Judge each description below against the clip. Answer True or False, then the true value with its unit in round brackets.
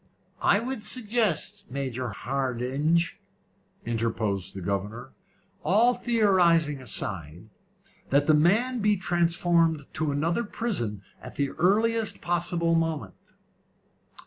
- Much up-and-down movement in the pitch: True (8.3 semitones)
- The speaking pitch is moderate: True (165 Hz)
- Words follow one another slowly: True (100 wpm)